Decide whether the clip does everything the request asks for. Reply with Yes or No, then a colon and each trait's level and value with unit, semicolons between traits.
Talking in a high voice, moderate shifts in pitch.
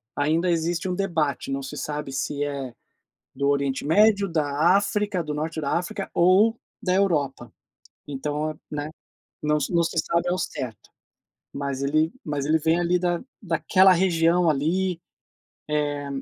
No: medium, 160 Hz; average, 3.6 semitones